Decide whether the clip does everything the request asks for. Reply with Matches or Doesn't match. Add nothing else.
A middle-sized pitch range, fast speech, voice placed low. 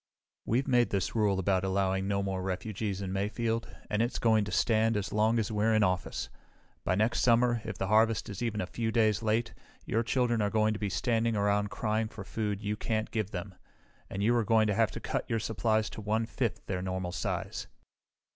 Doesn't match